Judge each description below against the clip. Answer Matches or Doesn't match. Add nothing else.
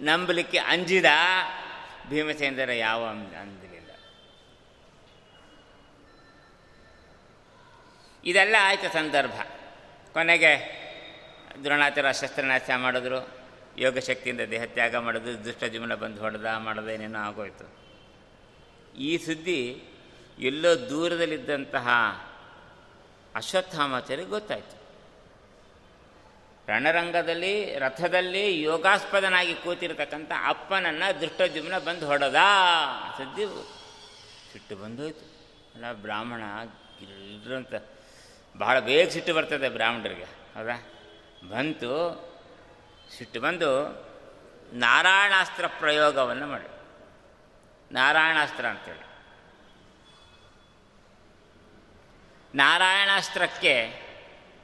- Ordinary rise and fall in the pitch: Doesn't match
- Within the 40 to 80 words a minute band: Matches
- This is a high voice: Doesn't match